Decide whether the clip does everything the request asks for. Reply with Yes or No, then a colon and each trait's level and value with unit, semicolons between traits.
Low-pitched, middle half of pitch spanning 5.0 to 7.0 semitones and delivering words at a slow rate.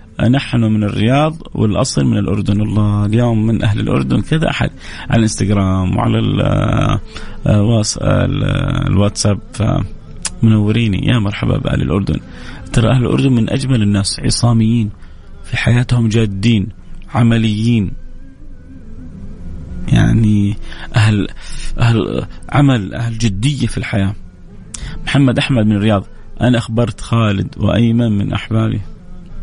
No: low, 110 Hz; average, 3.0 semitones; slow, 105 wpm